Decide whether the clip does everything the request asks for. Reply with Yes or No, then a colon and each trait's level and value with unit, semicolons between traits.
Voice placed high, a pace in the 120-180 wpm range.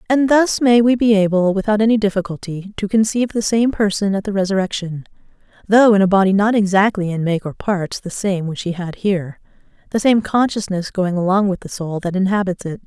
No: high, 200 Hz; average, 200 wpm